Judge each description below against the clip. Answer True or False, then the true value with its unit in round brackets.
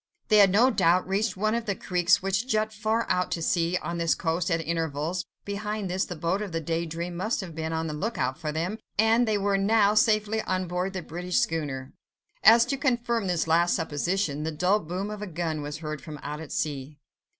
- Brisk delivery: True (230 wpm)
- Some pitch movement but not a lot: True (4.6 semitones)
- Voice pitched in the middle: True (180 Hz)